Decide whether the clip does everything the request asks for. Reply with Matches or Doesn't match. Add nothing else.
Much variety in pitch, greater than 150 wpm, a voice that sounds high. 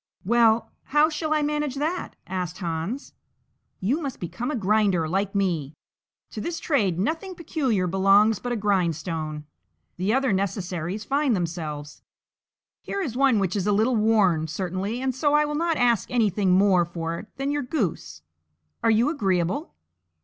Matches